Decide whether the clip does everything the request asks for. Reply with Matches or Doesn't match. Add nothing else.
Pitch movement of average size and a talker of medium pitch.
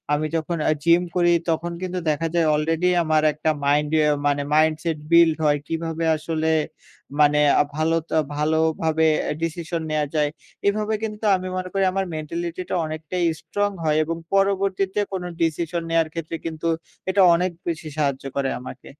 Doesn't match